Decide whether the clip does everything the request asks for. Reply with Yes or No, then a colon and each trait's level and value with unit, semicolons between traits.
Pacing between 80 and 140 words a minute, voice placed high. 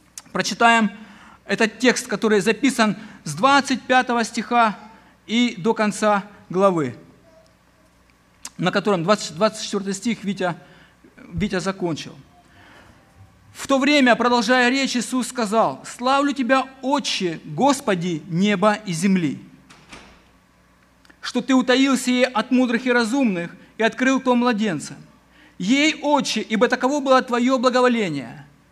Yes: average, 110 wpm; high, 225 Hz